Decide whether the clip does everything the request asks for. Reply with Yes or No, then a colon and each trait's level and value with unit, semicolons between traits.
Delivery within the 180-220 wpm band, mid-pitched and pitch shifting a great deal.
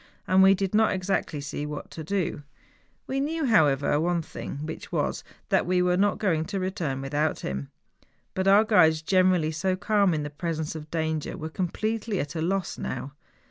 No: average, 190 wpm; medium, 175 Hz; average, 4.0 semitones